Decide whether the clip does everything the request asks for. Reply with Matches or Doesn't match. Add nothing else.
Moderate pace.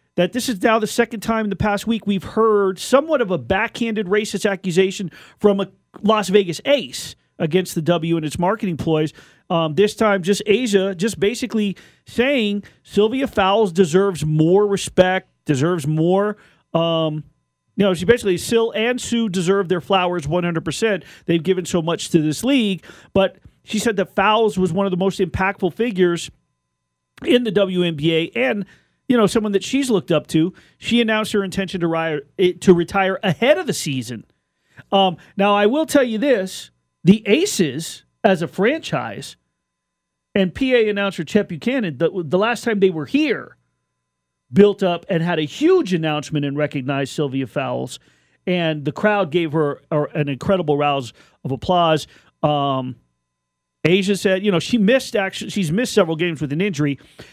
Matches